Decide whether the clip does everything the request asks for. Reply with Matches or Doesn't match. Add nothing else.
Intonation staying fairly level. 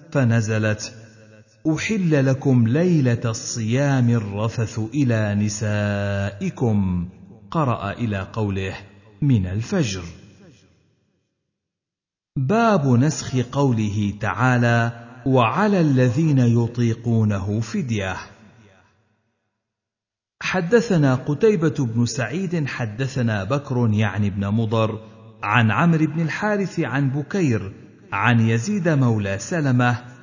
Doesn't match